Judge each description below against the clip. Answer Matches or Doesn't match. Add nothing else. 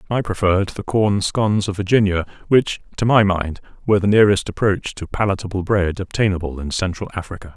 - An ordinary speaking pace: Matches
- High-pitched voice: Doesn't match